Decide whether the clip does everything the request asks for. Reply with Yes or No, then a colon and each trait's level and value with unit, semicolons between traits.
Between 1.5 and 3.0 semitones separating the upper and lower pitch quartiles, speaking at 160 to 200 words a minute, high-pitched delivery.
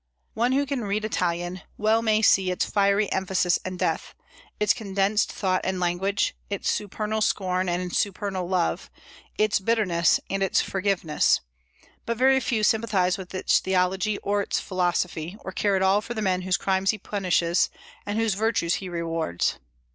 Yes: average, 2.7 semitones; average, 165 wpm; high, 195 Hz